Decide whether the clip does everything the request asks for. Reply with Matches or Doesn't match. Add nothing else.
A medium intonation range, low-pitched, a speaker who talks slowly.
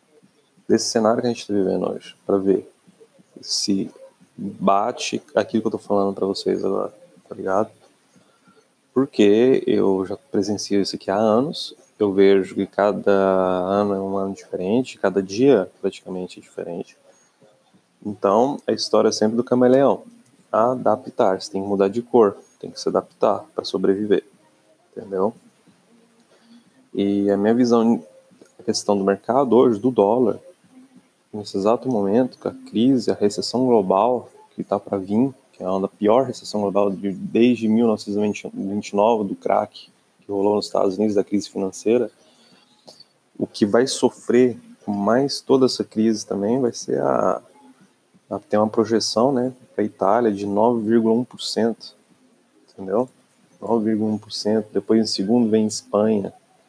Doesn't match